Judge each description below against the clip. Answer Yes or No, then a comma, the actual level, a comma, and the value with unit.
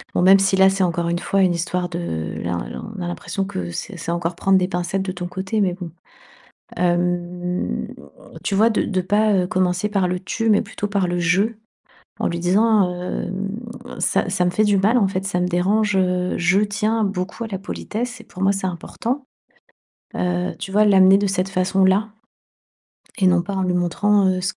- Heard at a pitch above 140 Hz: Yes, medium, 185 Hz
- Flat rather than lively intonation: Yes, narrow, 2.1 semitones